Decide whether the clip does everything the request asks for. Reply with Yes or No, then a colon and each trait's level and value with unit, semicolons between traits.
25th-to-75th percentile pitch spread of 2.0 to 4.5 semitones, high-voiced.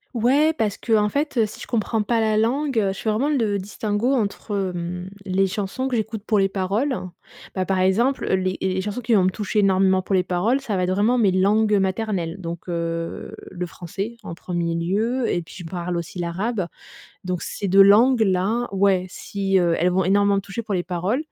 Yes: average, 3.3 semitones; high, 200 Hz